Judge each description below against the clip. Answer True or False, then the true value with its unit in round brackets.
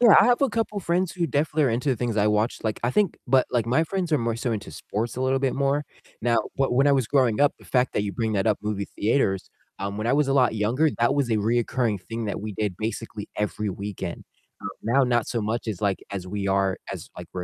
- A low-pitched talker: True (115 Hz)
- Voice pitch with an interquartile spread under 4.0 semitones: False (4.6 semitones)